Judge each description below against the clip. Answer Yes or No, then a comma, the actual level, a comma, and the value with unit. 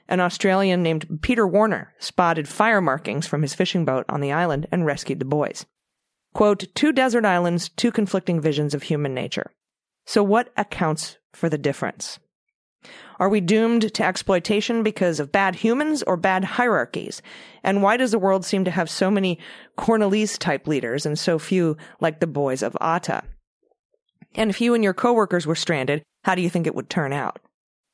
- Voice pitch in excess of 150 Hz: Yes, medium, 185 Hz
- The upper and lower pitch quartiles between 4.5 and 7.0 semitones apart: Yes, average, 5.2 semitones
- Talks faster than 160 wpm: Yes, average, 180 wpm